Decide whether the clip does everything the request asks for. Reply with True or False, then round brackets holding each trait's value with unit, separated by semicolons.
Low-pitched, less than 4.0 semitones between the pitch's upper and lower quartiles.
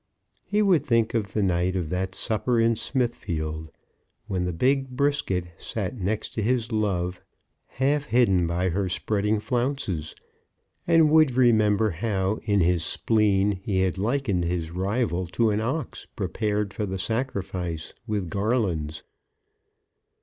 False (105 Hz; 4.6 semitones)